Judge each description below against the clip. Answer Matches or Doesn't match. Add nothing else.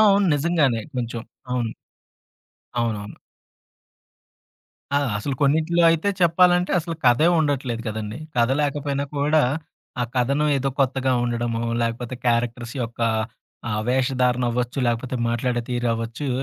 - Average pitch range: Matches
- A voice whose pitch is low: Matches